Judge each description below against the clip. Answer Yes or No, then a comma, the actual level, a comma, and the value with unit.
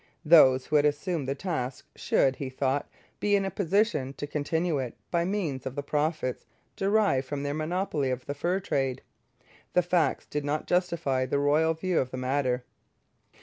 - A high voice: No, medium, 145 Hz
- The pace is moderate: Yes, average, 180 wpm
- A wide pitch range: No, average, 4.4 semitones